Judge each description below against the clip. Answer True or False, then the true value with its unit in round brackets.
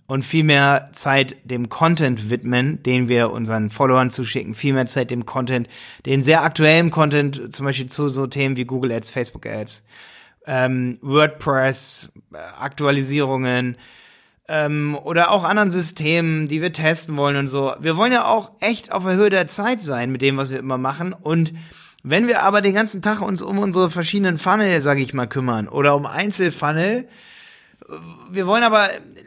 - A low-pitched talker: False (145 Hz)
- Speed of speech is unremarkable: True (175 wpm)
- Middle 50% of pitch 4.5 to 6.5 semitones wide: True (5.0 semitones)